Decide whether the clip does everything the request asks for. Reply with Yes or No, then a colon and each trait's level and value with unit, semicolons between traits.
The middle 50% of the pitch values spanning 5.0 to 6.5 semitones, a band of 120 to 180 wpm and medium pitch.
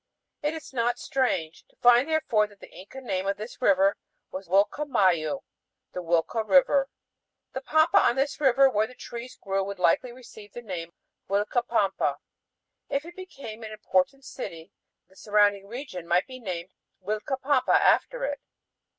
No: wide, 5.6 semitones; average, 165 wpm; high, 220 Hz